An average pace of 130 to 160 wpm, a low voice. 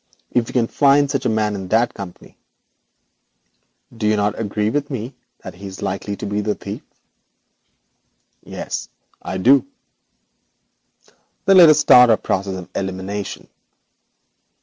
Yes: average, 145 wpm; low, 105 Hz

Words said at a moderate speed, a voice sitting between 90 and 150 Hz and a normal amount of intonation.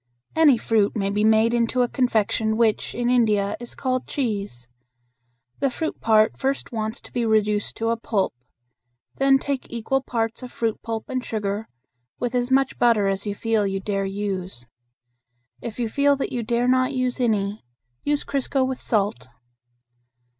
No: average, 170 wpm; high, 230 Hz; average, 3.4 semitones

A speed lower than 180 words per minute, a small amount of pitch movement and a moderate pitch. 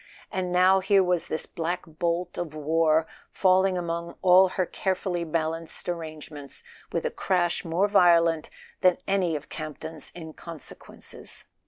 Yes: average, 140 wpm; narrow, 2.3 semitones; medium, 170 Hz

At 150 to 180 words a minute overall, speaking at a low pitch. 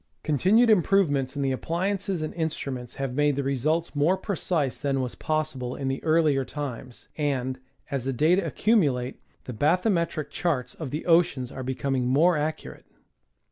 No: average, 165 wpm; medium, 145 Hz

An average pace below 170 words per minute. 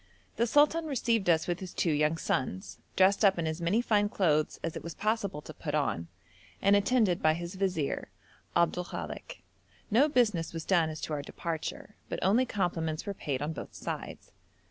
No: average, 190 wpm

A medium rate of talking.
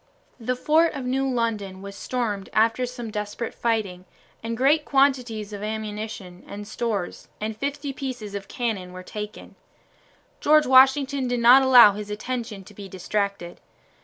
Yes: average, 145 wpm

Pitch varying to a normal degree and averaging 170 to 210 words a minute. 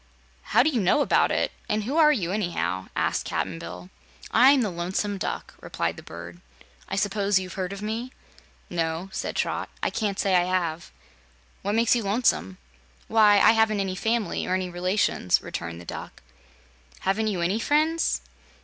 Yes: average, 4.2 semitones; average, 175 wpm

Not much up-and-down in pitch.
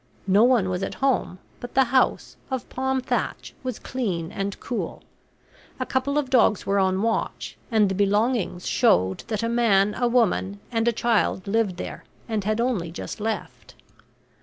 No: average, 4.0 semitones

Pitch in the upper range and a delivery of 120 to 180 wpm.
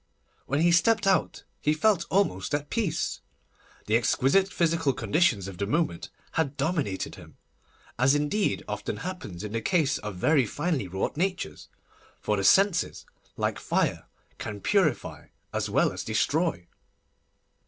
No: medium, 150 Hz; average, 145 wpm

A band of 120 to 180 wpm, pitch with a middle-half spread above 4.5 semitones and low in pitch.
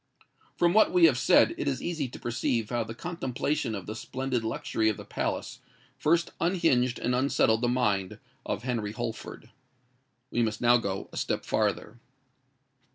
No: average, 165 wpm; average, 4.1 semitones; low, 120 Hz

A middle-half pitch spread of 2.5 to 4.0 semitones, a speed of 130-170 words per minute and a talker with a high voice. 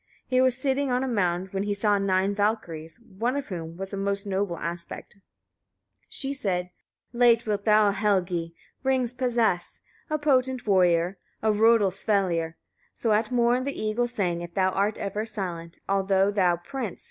No: average, 4.4 semitones; average, 165 wpm; high, 205 Hz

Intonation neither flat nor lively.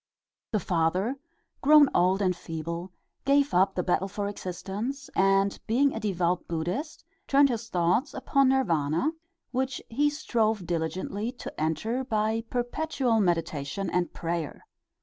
No: wide, 6.6 semitones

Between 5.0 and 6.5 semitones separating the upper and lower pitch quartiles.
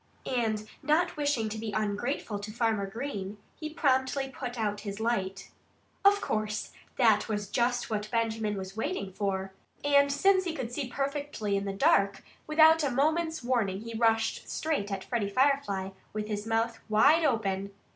Yes: average, 5.3 semitones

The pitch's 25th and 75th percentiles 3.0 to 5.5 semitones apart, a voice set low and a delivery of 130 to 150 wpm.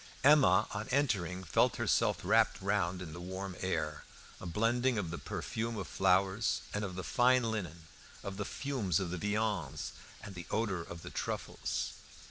No: average, 3.5 semitones; low, 100 Hz; average, 170 wpm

